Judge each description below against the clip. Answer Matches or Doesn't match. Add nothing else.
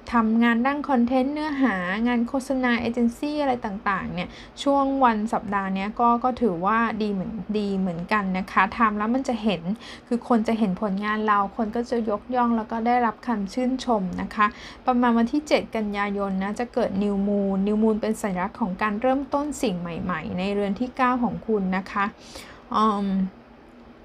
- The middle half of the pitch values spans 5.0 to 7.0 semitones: Doesn't match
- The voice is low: Doesn't match